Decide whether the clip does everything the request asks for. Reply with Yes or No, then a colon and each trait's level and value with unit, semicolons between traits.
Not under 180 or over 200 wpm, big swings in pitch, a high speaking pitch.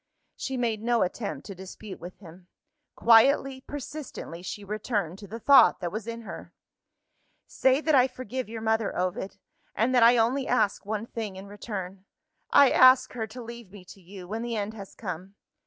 No: average, 185 wpm; average, 3.8 semitones; high, 220 Hz